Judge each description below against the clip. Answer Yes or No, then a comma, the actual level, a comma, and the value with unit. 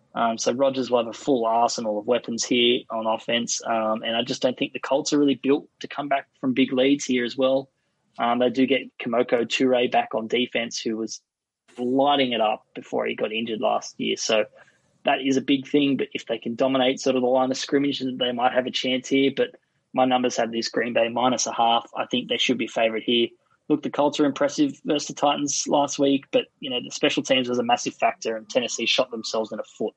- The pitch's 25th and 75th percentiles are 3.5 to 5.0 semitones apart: No, average, 2.8 semitones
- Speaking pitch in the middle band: No, low, 130 Hz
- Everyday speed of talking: No, fast, 240 wpm